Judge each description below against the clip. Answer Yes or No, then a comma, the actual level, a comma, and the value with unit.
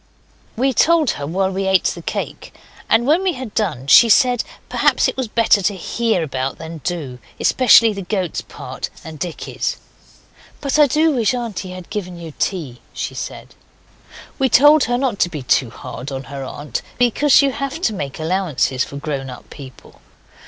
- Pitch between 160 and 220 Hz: Yes, high, 190 Hz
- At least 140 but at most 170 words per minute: No, average, 180 wpm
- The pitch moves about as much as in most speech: No, wide, 8.6 semitones